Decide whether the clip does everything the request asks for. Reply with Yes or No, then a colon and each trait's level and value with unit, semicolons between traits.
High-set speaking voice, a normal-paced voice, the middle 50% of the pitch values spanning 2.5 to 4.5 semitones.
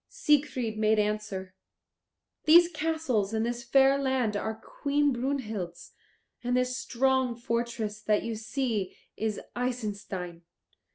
No: high, 235 Hz; slow, 115 wpm; average, 3.8 semitones